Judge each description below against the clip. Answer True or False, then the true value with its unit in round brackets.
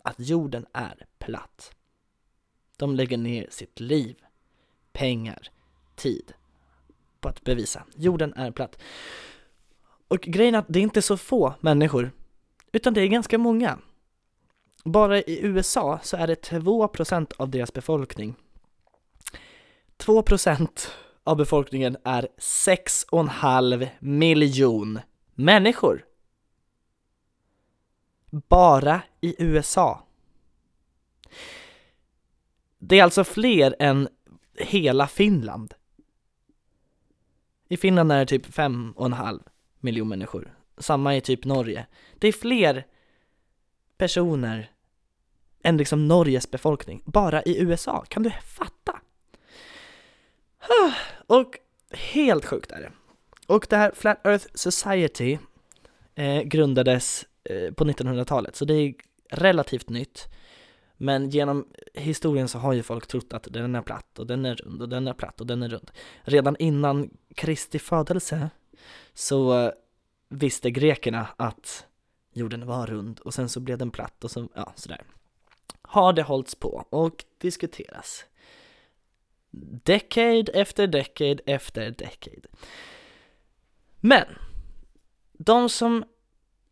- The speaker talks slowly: True (115 wpm)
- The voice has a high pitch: False (140 Hz)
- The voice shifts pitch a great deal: True (6.5 semitones)